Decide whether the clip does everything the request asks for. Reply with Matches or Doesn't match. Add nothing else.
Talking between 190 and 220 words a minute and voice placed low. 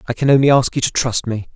Doesn't match